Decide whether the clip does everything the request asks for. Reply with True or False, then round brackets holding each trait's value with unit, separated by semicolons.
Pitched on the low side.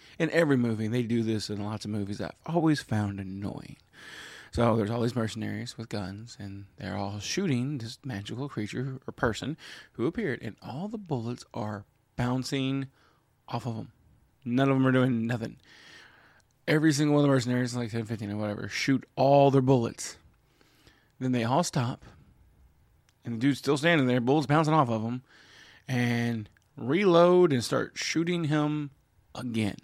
True (120 Hz)